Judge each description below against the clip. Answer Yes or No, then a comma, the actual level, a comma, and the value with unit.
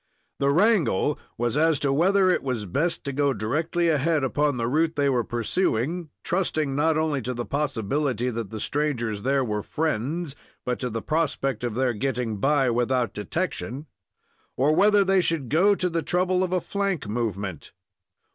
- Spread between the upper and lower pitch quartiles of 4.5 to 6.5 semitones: Yes, wide, 5.5 semitones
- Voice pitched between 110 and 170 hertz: Yes, medium, 140 Hz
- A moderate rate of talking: Yes, average, 175 wpm